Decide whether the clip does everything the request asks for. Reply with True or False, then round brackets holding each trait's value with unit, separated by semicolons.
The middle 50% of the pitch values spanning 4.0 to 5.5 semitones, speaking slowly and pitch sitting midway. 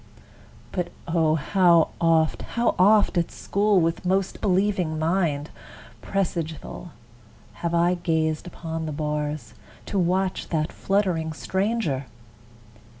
False (3.1 semitones; 110 wpm; 170 Hz)